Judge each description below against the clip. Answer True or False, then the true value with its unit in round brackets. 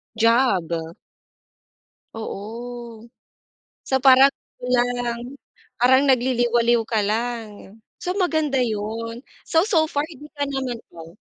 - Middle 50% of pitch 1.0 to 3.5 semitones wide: True (2.9 semitones)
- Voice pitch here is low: False (245 Hz)